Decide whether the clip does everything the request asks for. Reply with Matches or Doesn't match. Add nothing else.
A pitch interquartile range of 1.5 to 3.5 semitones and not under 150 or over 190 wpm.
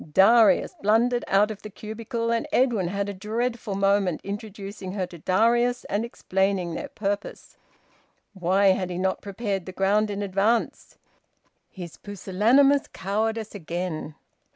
Doesn't match